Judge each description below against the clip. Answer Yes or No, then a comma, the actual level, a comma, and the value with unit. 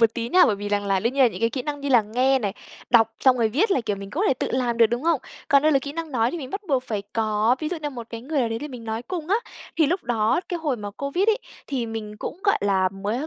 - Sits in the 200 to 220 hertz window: No, high, 245 Hz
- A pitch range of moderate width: Yes, average, 4.8 semitones